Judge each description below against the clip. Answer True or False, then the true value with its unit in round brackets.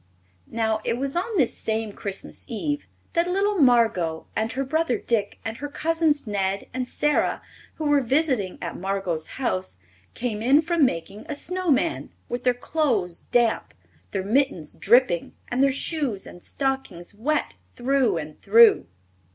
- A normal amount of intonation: False (6.4 semitones)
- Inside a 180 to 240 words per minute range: False (155 wpm)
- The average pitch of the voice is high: True (245 Hz)